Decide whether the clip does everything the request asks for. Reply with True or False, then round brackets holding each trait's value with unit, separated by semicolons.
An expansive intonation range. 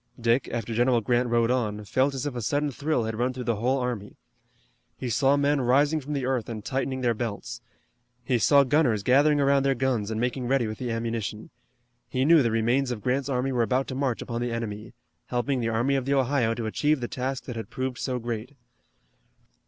False (2.7 semitones)